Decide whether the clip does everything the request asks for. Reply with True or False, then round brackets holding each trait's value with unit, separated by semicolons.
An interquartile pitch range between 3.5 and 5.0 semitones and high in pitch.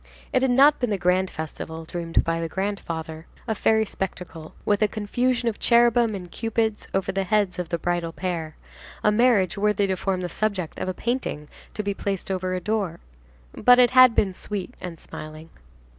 True (4.1 semitones; 195 Hz)